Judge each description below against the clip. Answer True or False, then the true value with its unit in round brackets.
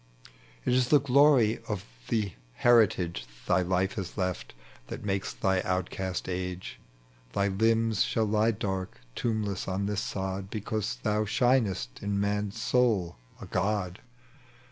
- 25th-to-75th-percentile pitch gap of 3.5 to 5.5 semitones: False (3.0 semitones)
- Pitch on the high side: False (100 Hz)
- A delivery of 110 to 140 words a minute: True (135 wpm)